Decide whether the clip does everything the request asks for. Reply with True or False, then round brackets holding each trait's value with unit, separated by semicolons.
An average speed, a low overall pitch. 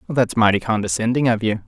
True (180 wpm; 115 Hz)